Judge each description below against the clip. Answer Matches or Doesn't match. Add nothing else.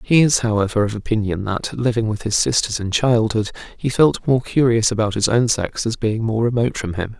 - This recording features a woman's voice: Doesn't match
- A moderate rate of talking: Doesn't match